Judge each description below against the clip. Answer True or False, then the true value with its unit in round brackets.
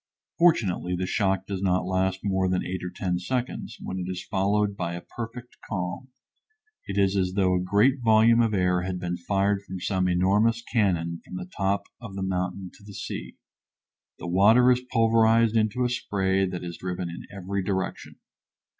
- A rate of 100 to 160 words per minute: False (185 wpm)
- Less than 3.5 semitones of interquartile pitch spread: True (2.9 semitones)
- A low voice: True (95 Hz)